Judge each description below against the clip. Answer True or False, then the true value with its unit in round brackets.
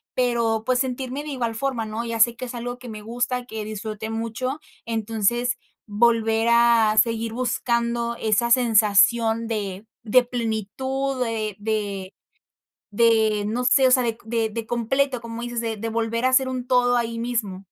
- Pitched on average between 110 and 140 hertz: False (230 Hz)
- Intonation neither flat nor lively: False (1.9 semitones)